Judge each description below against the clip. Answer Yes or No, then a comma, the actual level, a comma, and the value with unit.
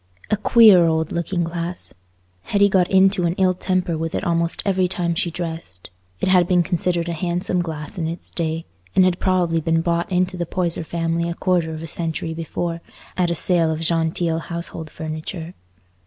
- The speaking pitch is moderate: Yes, medium, 170 Hz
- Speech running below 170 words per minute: No, average, 185 wpm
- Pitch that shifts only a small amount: Yes, narrow, 1.8 semitones